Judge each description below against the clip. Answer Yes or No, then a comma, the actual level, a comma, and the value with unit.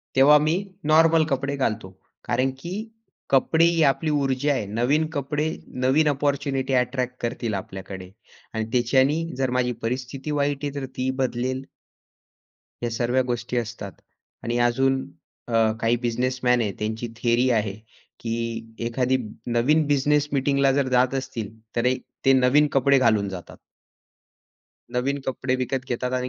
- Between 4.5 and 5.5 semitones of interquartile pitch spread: No, average, 2.9 semitones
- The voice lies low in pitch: Yes, low, 130 Hz